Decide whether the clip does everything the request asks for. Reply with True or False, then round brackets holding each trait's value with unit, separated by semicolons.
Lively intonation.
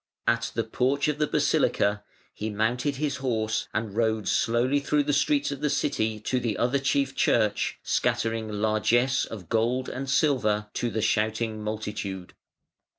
False (4.0 semitones)